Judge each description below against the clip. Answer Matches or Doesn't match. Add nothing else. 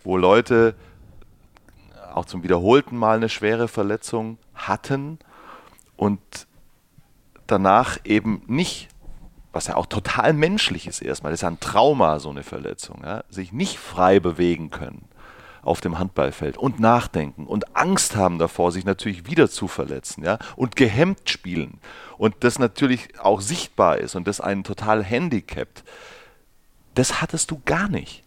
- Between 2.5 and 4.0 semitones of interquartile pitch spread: Doesn't match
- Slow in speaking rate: Doesn't match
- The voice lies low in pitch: Matches